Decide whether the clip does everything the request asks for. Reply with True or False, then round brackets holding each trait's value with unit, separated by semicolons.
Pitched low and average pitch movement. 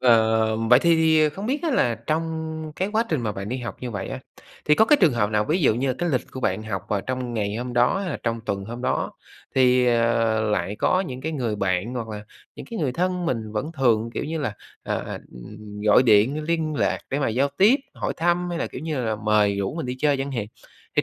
False (125 Hz; 6.4 semitones)